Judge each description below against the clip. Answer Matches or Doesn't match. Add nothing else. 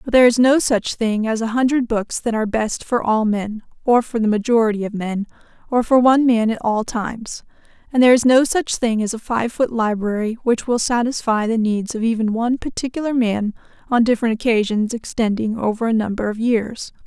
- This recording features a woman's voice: Matches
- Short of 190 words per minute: Doesn't match